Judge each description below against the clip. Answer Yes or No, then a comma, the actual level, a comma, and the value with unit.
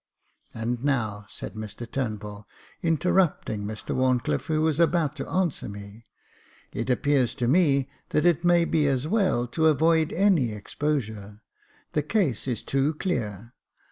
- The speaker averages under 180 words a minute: Yes, average, 150 wpm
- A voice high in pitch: No, low, 135 Hz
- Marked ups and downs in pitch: Yes, wide, 6.4 semitones